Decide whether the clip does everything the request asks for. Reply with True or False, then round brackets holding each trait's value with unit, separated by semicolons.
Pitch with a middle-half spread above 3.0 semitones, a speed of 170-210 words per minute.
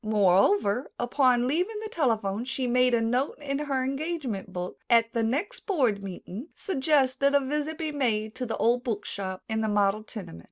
True (4.8 semitones; 190 wpm)